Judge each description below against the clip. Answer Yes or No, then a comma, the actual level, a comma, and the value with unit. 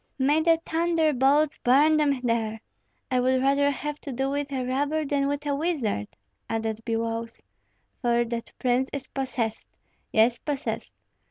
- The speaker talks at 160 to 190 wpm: No, average, 150 wpm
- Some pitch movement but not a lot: Yes, average, 3.5 semitones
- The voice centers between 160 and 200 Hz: No, very high, 270 Hz